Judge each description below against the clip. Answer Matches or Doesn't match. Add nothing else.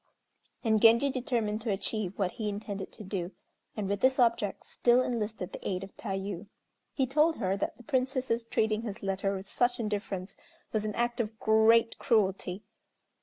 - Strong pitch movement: Doesn't match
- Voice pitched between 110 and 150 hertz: Doesn't match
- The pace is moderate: Matches